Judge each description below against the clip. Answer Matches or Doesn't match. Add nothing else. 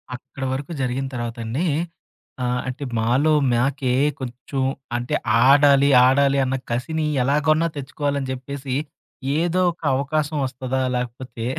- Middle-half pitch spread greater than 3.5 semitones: Doesn't match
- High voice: Doesn't match